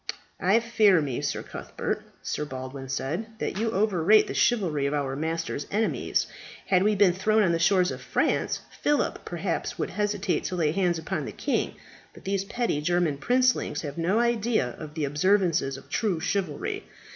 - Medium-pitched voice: Yes, medium, 180 Hz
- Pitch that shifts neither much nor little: No, wide, 5.8 semitones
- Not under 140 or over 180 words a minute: Yes, average, 175 wpm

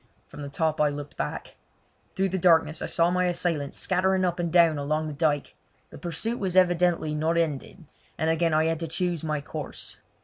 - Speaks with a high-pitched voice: No, medium, 165 Hz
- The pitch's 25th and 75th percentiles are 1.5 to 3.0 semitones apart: Yes, narrow, 2.5 semitones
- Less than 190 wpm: No, average, 200 wpm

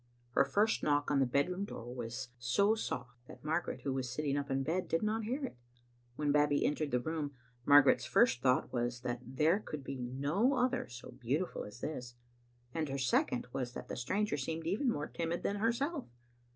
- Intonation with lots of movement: Yes, wide, 6.3 semitones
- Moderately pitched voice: Yes, medium, 145 Hz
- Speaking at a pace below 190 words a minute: No, average, 195 wpm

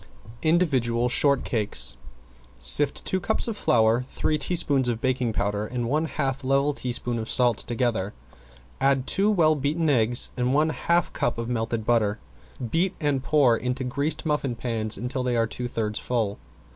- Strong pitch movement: No, average, 4.0 semitones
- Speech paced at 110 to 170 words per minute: Yes, average, 160 wpm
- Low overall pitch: Yes, low, 125 Hz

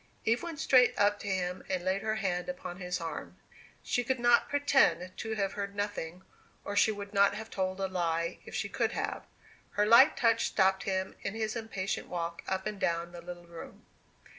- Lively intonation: No, average, 3.6 semitones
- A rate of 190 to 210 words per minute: Yes, average, 195 wpm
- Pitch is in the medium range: No, high, 200 Hz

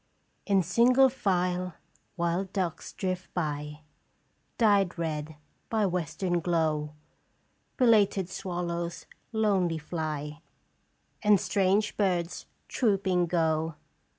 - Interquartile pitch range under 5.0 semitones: Yes, average, 3.3 semitones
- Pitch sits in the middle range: Yes, medium, 180 Hz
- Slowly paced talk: Yes, slow, 95 wpm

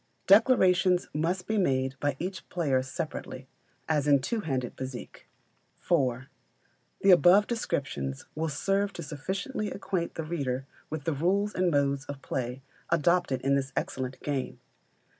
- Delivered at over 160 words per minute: No, average, 140 wpm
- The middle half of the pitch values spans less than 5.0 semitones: No, wide, 5.4 semitones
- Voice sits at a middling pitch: Yes, medium, 155 Hz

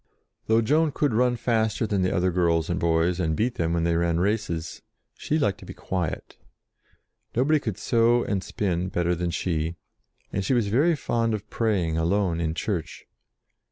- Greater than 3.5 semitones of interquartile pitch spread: Yes, average, 5.2 semitones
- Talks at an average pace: Yes, average, 190 wpm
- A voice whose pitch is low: Yes, very low, 95 Hz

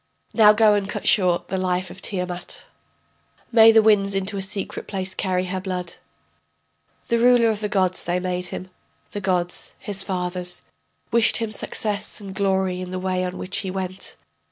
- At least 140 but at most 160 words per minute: No, average, 180 wpm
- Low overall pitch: No, high, 190 Hz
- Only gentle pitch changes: Yes, narrow, 2.1 semitones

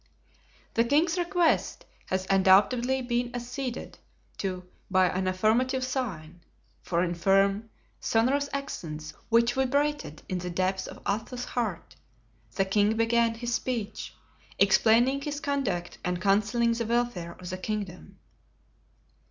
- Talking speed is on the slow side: Yes, slow, 125 wpm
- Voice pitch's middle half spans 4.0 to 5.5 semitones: Yes, average, 5.1 semitones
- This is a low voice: No, high, 225 Hz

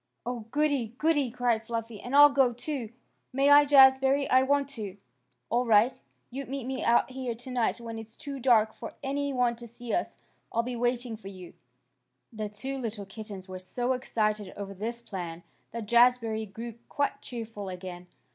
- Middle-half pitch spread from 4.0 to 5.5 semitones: No, average, 3.5 semitones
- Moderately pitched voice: No, high, 235 Hz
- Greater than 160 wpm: Yes, average, 175 wpm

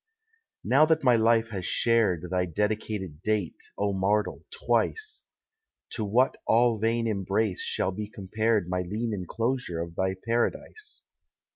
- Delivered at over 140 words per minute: No, slow, 135 wpm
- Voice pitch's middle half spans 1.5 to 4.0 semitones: Yes, average, 3.6 semitones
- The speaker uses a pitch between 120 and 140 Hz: No, low, 110 Hz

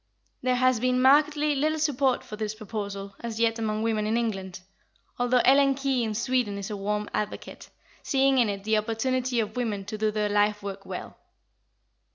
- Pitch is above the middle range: Yes, high, 225 Hz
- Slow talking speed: No, average, 185 wpm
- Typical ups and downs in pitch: Yes, average, 3.4 semitones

